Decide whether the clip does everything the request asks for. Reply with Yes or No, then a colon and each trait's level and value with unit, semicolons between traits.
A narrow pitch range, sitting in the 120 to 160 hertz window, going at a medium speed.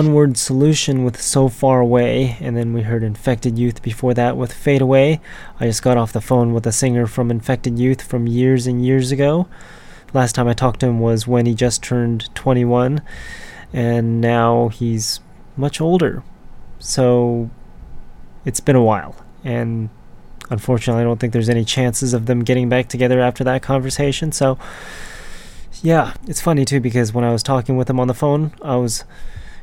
Yes: narrow, 1.9 semitones; low, 125 Hz; average, 185 wpm